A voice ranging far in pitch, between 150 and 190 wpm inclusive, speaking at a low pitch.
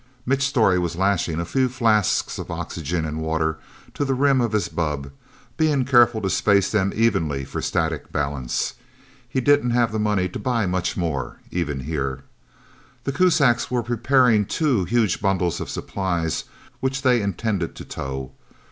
Yes: wide, 7.0 semitones; average, 165 wpm; low, 100 Hz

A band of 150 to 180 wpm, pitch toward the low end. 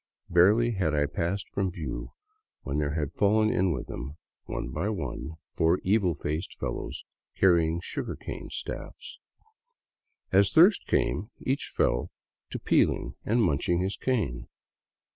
No: slow, 135 wpm; very low, 90 Hz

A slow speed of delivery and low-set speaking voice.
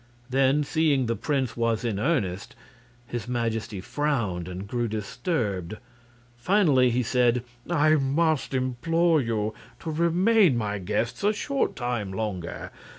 Yes: slow, 130 wpm; low, 125 Hz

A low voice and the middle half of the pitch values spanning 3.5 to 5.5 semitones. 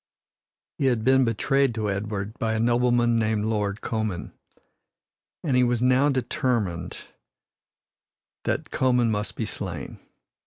No: low, 115 Hz; average, 3.1 semitones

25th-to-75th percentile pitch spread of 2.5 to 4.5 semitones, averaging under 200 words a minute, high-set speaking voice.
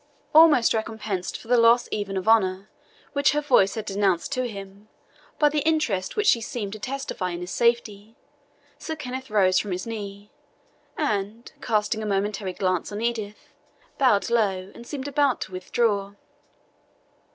Yes: average, 3.9 semitones; average, 160 wpm; high, 215 Hz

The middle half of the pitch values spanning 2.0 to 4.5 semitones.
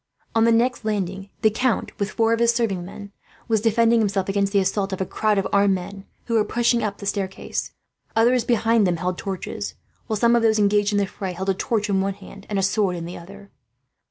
Yes: narrow, 2.6 semitones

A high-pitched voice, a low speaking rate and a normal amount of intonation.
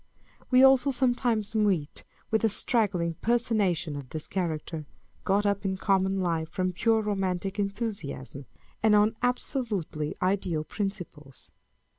Yes: high, 195 Hz; slow, 125 wpm; average, 4.6 semitones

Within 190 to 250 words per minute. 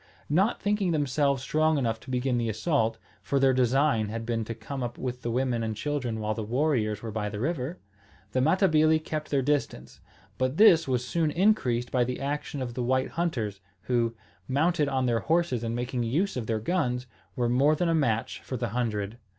Yes: average, 200 wpm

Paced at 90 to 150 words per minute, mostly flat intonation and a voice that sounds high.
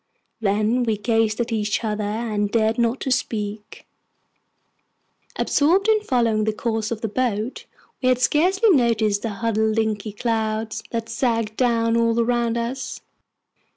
Yes: average, 140 wpm; narrow, 1.9 semitones; high, 230 Hz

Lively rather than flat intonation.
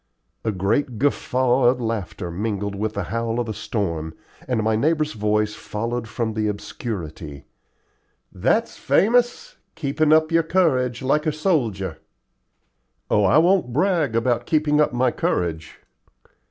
Yes: wide, 6.4 semitones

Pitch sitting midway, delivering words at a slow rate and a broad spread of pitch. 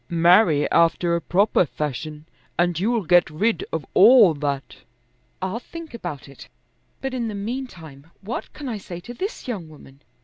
No: medium, 175 Hz; average, 165 wpm; wide, 6.9 semitones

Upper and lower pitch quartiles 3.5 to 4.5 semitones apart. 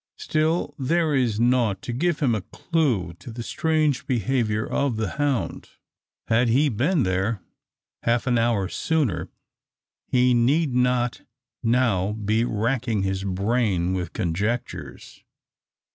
Yes: average, 4.2 semitones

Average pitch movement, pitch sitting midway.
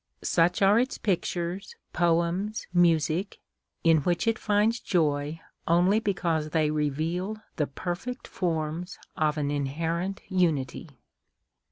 Yes: average, 3.7 semitones; medium, 170 Hz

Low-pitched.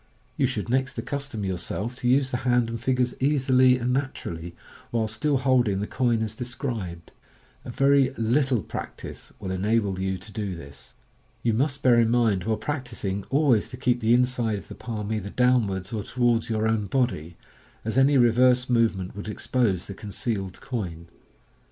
Yes: low, 115 Hz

